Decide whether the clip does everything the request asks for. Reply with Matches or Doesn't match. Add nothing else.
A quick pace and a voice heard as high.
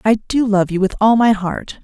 Matches